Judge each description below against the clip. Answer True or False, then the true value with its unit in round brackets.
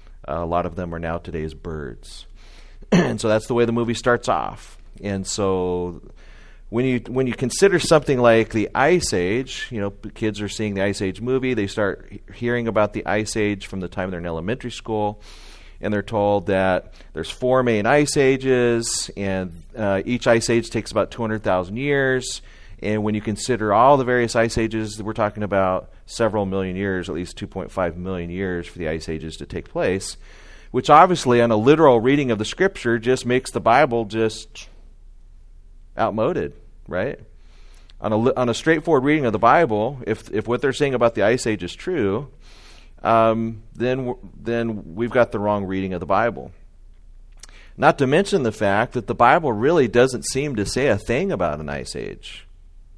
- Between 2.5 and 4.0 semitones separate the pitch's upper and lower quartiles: False (4.5 semitones)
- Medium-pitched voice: False (110 Hz)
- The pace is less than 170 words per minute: False (195 wpm)